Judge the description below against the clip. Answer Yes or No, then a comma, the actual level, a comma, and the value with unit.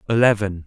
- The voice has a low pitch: Yes, low, 100 Hz